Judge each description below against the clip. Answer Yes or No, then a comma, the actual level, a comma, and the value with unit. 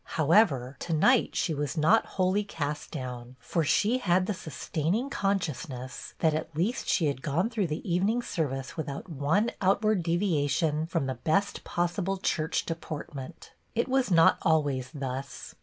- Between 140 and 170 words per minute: Yes, average, 165 wpm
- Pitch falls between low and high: Yes, medium, 165 Hz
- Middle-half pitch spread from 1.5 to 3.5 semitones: No, average, 5.3 semitones